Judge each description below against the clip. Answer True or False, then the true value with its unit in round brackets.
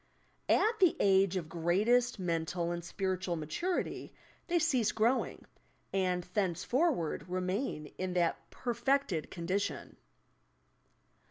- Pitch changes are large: True (5.9 semitones)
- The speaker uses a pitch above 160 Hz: True (190 Hz)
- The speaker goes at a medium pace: False (100 wpm)